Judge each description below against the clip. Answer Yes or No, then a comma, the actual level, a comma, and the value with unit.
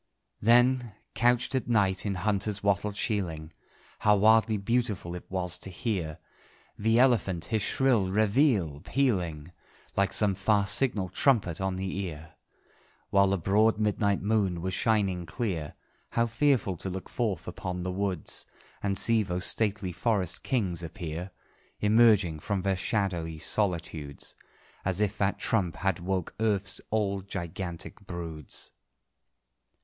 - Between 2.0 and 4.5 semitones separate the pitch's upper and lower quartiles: Yes, average, 3.4 semitones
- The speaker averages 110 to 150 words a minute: Yes, slow, 135 wpm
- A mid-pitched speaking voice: No, low, 100 Hz